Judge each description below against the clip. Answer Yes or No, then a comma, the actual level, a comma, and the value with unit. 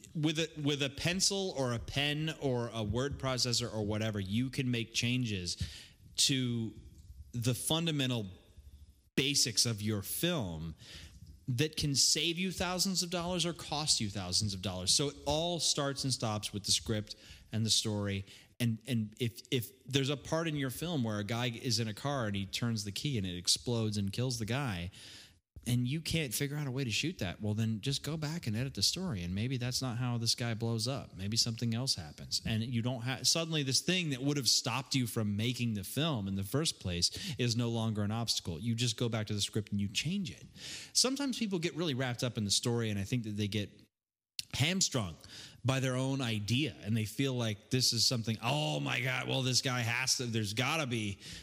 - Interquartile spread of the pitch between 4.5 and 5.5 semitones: Yes, average, 4.8 semitones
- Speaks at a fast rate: Yes, fast, 215 wpm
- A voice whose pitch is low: Yes, low, 120 Hz